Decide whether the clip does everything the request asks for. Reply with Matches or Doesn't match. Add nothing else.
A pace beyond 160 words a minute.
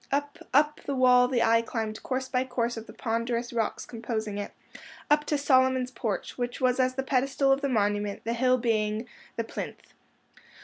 Matches